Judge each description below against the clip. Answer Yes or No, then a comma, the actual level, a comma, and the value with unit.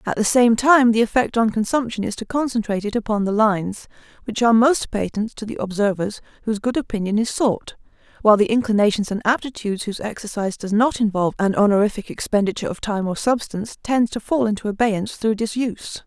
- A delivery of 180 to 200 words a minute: Yes, average, 190 wpm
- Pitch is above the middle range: Yes, high, 220 Hz